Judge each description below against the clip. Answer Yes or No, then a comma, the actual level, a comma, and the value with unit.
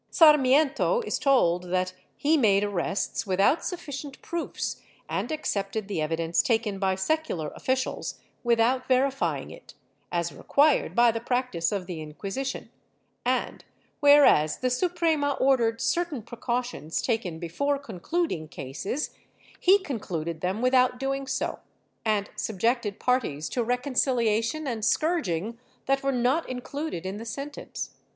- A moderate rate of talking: No, slow, 130 wpm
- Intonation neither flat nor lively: No, wide, 6.1 semitones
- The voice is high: Yes, high, 240 Hz